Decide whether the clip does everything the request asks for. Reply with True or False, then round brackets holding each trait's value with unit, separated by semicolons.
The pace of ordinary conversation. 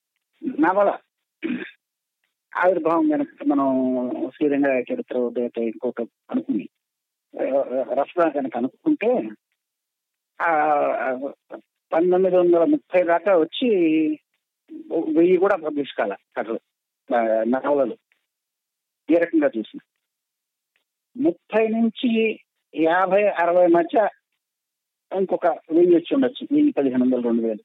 True (85 wpm)